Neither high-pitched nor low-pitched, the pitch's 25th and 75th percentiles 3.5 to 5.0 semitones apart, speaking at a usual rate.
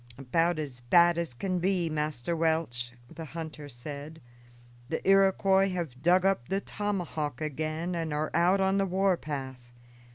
Yes: medium, 165 Hz; average, 3.8 semitones; average, 155 wpm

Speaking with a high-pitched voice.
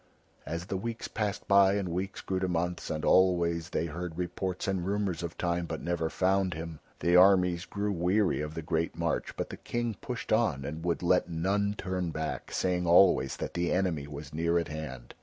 No: very low, 90 Hz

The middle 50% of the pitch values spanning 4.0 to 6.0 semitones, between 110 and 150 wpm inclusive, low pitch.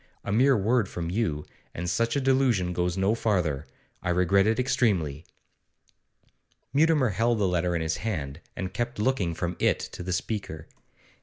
No: average, 4.9 semitones; average, 165 wpm; very low, 95 Hz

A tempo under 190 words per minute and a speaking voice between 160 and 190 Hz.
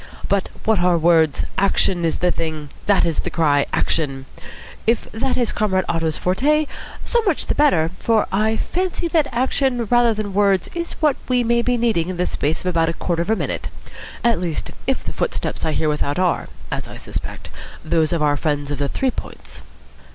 No: average, 200 wpm; medium, 185 Hz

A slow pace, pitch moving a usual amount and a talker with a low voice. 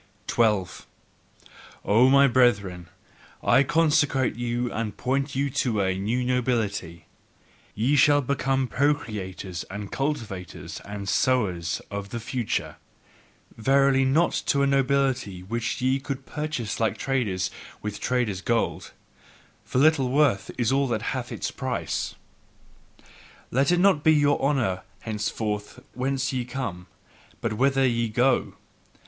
Yes: slow, 130 wpm; average, 4.5 semitones; low, 125 Hz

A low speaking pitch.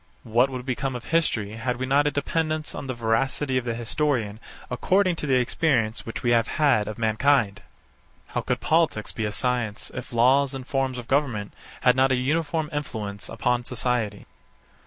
Yes: low, 125 Hz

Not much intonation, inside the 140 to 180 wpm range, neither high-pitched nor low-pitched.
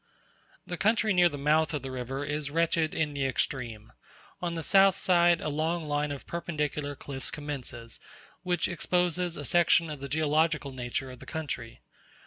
No: average, 3.6 semitones; average, 170 wpm; medium, 150 Hz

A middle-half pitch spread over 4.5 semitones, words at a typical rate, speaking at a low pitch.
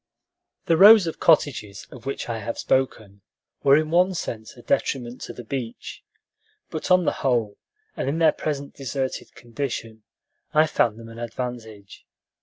Yes: average, 5.1 semitones; average, 160 wpm; low, 130 Hz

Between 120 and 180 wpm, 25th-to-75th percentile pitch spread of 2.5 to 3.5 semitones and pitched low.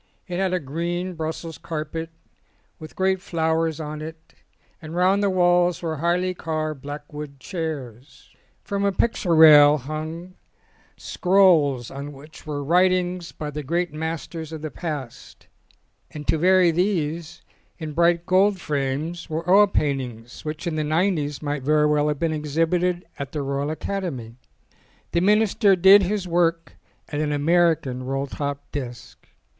No: average, 150 wpm; average, 3.2 semitones; medium, 160 Hz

